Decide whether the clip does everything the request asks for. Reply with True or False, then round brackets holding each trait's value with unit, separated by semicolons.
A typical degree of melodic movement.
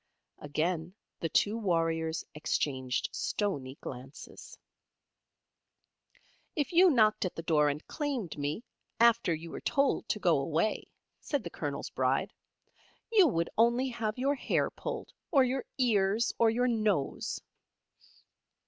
False (7.4 semitones)